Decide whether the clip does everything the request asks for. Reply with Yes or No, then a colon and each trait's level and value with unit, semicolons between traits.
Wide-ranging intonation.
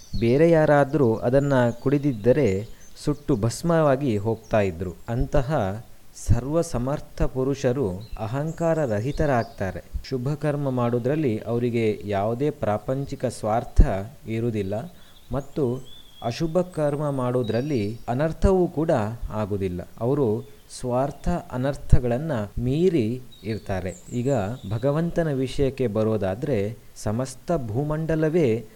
No: average, 4.9 semitones